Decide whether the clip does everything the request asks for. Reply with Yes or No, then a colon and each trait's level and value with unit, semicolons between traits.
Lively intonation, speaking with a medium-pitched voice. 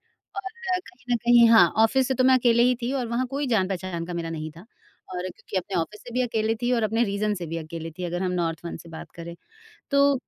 No: wide, 6.1 semitones; high, 220 Hz